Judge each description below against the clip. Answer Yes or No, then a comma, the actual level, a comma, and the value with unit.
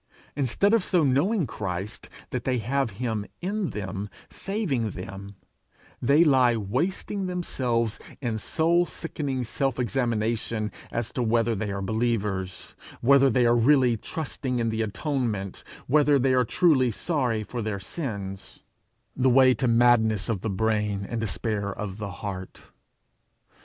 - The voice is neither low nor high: No, low, 120 Hz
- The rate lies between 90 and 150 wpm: Yes, average, 140 wpm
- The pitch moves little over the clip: No, average, 4.3 semitones